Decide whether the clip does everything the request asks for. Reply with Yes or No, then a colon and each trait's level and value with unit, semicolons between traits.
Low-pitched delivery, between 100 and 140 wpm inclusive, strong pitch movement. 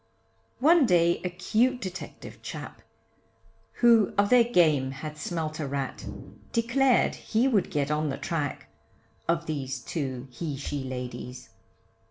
No: medium, 165 Hz; slow, 135 wpm; wide, 8.0 semitones